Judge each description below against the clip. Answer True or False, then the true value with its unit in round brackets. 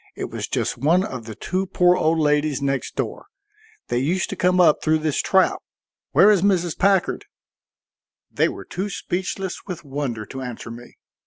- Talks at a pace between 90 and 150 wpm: False (175 wpm)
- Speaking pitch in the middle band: True (160 Hz)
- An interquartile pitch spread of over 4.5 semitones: True (5.0 semitones)